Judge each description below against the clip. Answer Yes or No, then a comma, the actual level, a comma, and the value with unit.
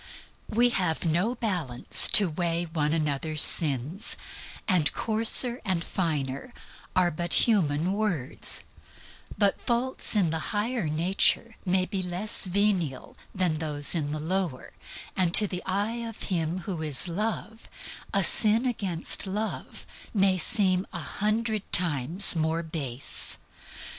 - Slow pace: Yes, slow, 130 wpm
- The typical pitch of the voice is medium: Yes, medium, 180 Hz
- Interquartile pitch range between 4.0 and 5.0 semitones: Yes, average, 4.7 semitones